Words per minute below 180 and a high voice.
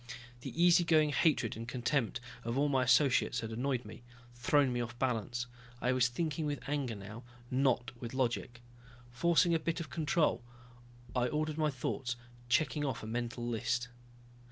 No: average, 165 wpm; low, 130 Hz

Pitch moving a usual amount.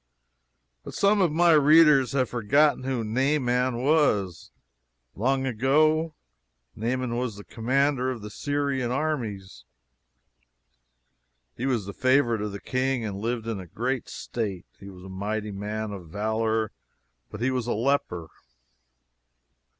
Yes: average, 4.4 semitones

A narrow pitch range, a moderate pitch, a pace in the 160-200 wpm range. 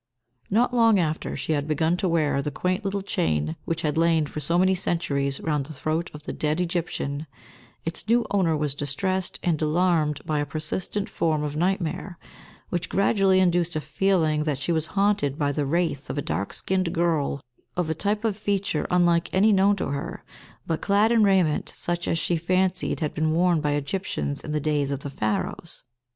No: average, 3.9 semitones; medium, 165 Hz; average, 195 wpm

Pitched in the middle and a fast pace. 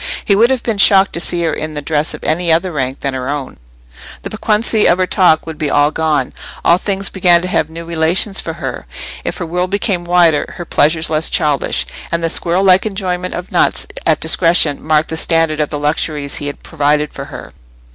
Yes: medium, 165 Hz; fast, 215 wpm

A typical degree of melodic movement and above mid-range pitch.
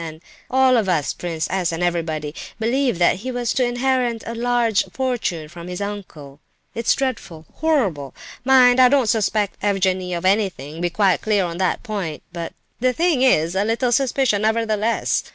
No: wide, 6.0 semitones; high, 210 Hz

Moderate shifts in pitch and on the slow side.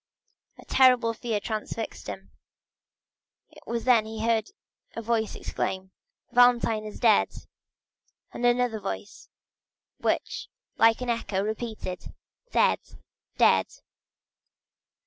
No: narrow, 2.0 semitones; slow, 100 wpm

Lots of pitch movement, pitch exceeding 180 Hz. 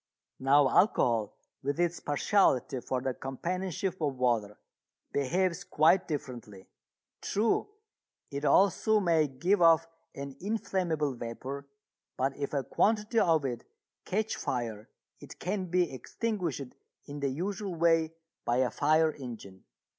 No: wide, 5.8 semitones; medium, 150 Hz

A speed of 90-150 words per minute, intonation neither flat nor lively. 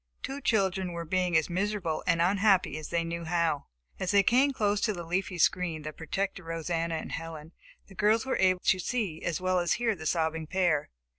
No: fast, 205 wpm; average, 3.1 semitones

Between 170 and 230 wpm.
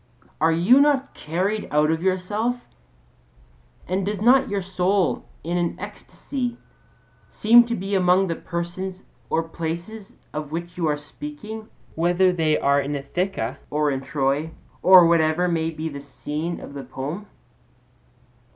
No: average, 145 wpm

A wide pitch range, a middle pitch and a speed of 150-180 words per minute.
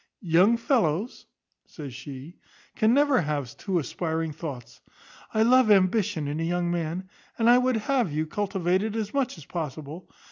Yes: wide, 6.1 semitones; medium, 180 Hz; average, 165 wpm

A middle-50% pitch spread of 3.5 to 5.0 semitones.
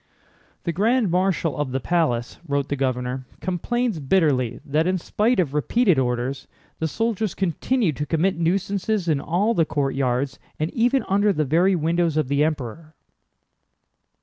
No: wide, 5.6 semitones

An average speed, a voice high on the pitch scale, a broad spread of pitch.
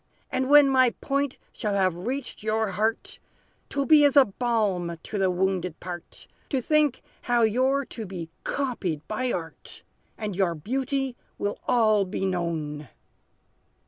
Yes: average, 150 wpm; high, 215 Hz; wide, 6.1 semitones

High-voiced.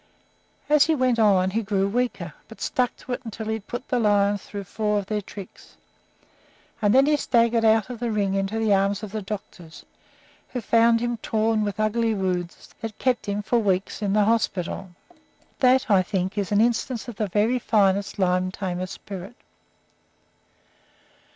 Yes: high, 215 Hz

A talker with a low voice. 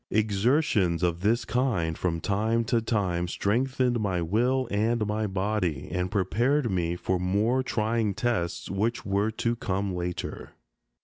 Yes: low, 105 Hz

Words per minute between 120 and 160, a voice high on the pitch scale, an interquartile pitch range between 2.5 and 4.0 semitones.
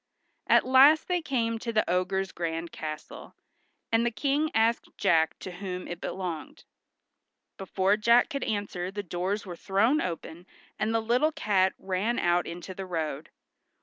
No: average, 155 wpm; high, 195 Hz; average, 4.6 semitones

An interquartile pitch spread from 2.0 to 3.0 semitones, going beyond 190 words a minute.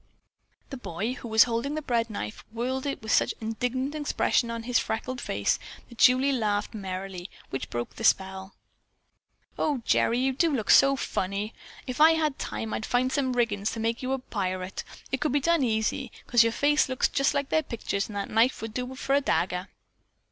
No: average, 3.8 semitones; average, 200 wpm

